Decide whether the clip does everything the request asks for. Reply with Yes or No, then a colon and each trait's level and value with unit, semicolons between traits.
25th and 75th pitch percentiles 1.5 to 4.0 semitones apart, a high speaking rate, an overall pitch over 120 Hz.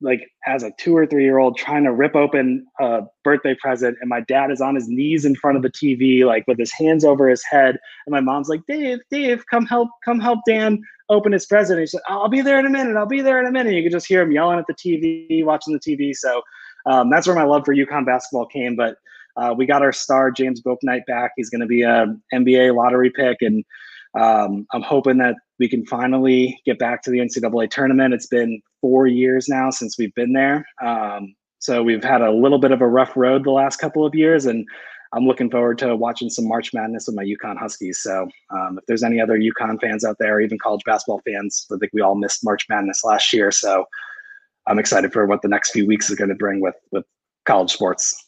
No: average, 4.5 semitones; fast, 240 wpm; low, 130 Hz